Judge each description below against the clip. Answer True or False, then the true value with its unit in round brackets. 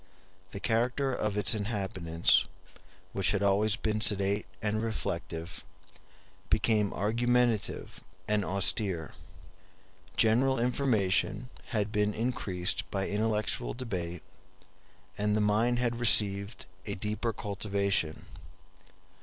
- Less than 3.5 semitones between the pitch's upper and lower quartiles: True (2.6 semitones)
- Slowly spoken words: True (100 wpm)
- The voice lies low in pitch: True (105 Hz)